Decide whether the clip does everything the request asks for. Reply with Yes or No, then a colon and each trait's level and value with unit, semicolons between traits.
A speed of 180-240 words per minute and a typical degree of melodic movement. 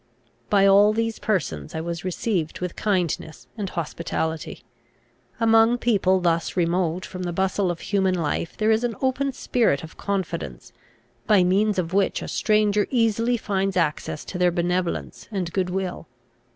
No: average, 155 wpm; average, 3.8 semitones